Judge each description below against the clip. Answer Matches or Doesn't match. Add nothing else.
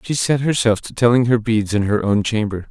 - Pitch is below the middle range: Matches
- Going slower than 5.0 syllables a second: Doesn't match